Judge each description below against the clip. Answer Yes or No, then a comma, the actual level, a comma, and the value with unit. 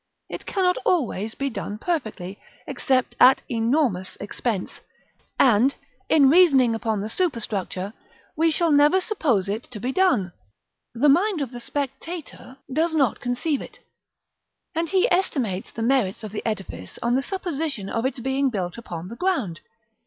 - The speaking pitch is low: No, very high, 255 Hz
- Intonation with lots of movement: Yes, wide, 6.6 semitones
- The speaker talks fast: No, average, 155 wpm